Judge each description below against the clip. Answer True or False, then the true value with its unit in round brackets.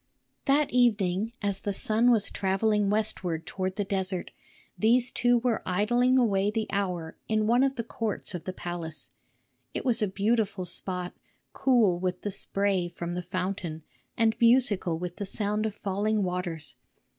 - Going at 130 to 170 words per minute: True (160 wpm)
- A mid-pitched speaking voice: False (200 Hz)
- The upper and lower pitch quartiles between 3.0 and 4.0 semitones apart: True (3.6 semitones)